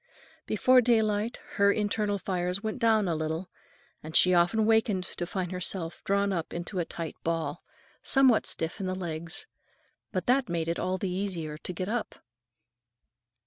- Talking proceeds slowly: No, average, 165 wpm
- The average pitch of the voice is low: No, medium, 185 Hz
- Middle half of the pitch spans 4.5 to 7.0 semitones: No, average, 3.8 semitones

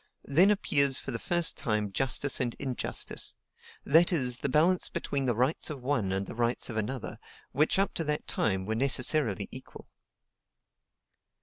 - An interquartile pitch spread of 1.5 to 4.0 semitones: No, average, 4.5 semitones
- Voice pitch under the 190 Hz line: Yes, low, 135 Hz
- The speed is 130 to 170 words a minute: Yes, average, 165 wpm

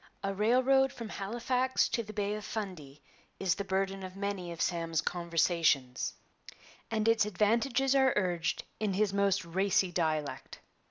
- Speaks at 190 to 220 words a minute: No, average, 150 wpm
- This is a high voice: Yes, high, 195 Hz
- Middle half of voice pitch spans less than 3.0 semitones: No, average, 4.0 semitones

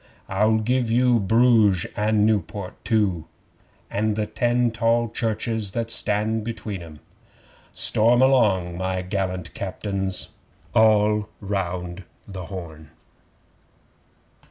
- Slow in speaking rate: Yes, slow, 105 wpm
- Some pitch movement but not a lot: Yes, average, 3.2 semitones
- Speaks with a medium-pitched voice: No, low, 105 Hz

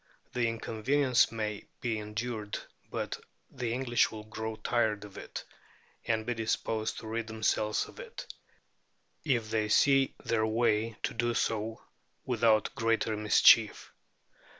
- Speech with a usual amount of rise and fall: No, narrow, 1.7 semitones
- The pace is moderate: No, slow, 130 wpm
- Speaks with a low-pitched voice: Yes, low, 110 Hz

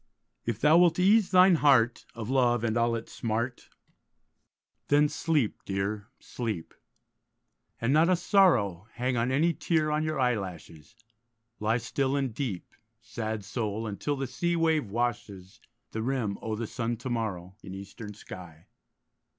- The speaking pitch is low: Yes, low, 120 Hz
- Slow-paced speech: No, average, 145 wpm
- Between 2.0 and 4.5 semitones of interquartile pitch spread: No, average, 5.3 semitones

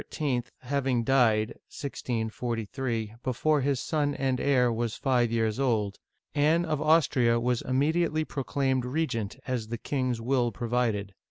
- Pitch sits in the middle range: No, low, 125 Hz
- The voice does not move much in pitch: No, average, 3.3 semitones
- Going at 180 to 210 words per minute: No, slow, 135 wpm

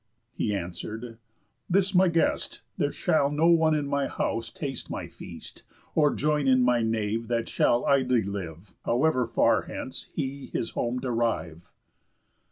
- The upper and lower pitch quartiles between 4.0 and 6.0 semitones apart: Yes, average, 4.6 semitones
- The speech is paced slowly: No, average, 150 wpm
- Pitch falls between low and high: No, low, 125 Hz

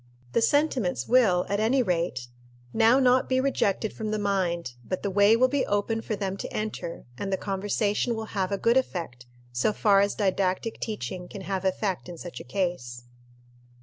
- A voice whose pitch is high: Yes, high, 200 Hz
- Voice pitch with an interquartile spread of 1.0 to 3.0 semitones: No, average, 3.6 semitones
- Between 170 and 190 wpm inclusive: Yes, average, 185 wpm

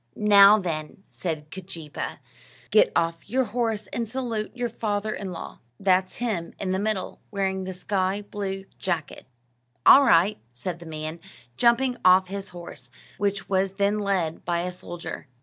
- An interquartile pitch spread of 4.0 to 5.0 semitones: No, average, 3.2 semitones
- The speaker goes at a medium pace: Yes, average, 155 wpm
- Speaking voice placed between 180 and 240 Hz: Yes, high, 190 Hz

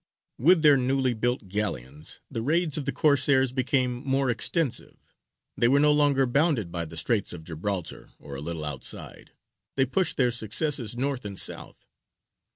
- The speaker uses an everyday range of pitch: No, wide, 5.9 semitones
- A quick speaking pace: No, average, 170 wpm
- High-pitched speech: No, low, 125 Hz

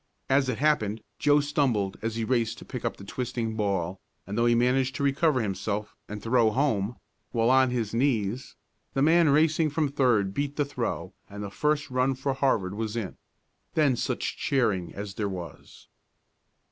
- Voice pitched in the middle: No, low, 120 Hz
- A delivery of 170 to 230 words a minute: Yes, average, 180 wpm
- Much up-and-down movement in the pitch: No, average, 4.9 semitones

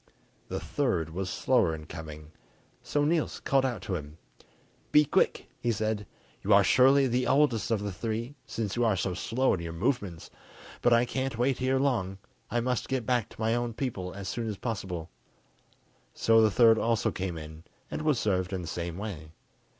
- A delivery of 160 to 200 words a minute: Yes, average, 190 wpm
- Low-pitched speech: Yes, low, 110 Hz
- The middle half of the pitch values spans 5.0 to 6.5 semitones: Yes, average, 5.3 semitones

